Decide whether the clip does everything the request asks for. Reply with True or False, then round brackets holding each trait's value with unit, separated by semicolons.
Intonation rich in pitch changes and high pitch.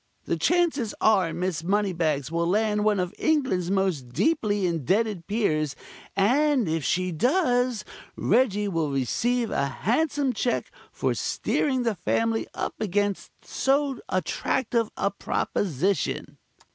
True (5.9 semitones; 205 Hz)